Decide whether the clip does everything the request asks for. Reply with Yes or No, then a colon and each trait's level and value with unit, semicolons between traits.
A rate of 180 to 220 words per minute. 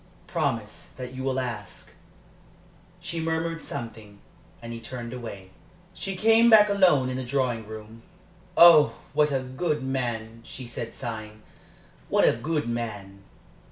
No: average, 140 wpm